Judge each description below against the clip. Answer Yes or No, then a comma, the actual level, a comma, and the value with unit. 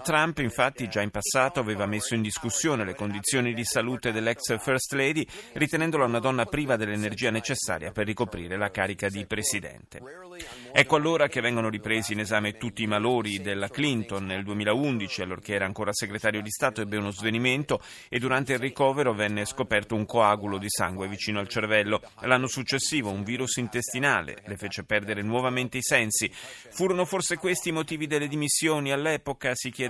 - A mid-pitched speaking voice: No, low, 115 Hz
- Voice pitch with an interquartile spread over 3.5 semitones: Yes, average, 4.4 semitones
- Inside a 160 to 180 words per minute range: Yes, fast, 170 wpm